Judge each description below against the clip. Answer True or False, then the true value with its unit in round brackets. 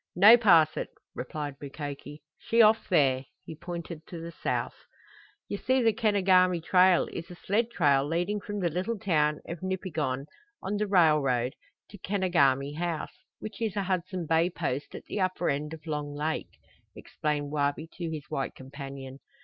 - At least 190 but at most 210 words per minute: False (165 wpm)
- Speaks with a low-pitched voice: False (165 Hz)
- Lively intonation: False (4.4 semitones)